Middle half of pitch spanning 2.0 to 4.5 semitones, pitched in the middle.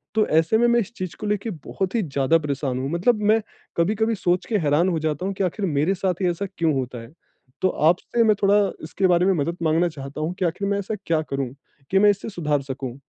No: average, 4.9 semitones; medium, 175 Hz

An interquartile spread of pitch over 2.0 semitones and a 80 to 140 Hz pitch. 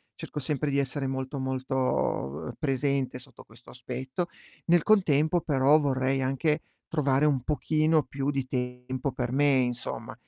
Yes: narrow, 2.4 semitones; low, 135 Hz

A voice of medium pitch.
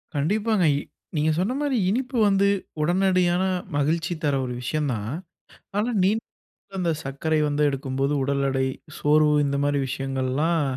Yes: medium, 150 Hz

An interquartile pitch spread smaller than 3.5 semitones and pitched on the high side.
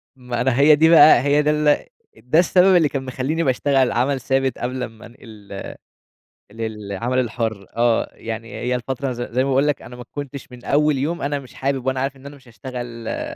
No: average, 2.9 semitones; low, 130 Hz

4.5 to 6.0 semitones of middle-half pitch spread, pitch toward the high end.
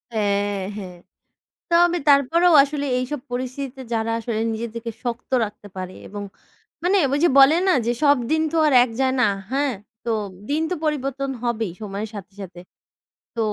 Yes: average, 5.2 semitones; very high, 250 Hz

